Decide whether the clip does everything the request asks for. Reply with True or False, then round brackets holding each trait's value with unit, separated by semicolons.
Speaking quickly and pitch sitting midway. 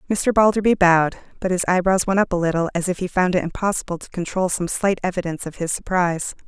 True (220 wpm; 180 Hz)